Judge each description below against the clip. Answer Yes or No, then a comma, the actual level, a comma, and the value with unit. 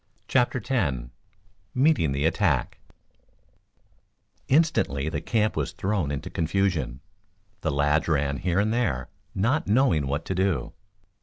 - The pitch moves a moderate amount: No, wide, 7.2 semitones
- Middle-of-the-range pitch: No, very low, 85 Hz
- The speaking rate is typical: No, slow, 125 wpm